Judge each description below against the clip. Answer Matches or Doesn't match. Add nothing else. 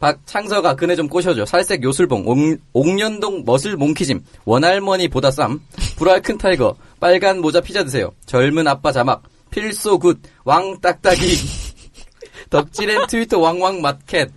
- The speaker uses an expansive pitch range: Doesn't match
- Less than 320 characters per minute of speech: Matches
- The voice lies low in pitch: Doesn't match